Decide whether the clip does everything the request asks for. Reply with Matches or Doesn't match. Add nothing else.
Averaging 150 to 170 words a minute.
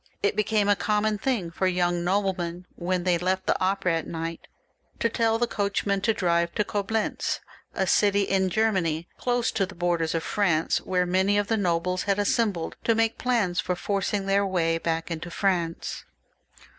Doesn't match